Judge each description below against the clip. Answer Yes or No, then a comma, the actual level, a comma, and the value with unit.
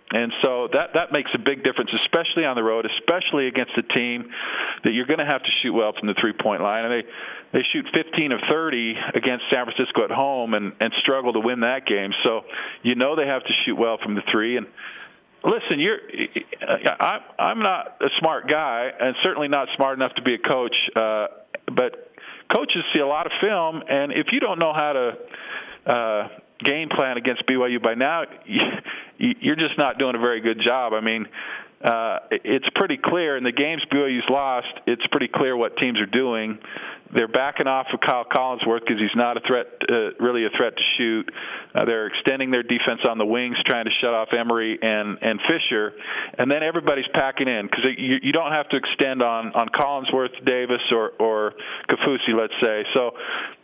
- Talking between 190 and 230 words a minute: Yes, average, 200 wpm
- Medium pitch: No, low, 130 Hz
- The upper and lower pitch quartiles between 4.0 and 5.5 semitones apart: Yes, average, 4.4 semitones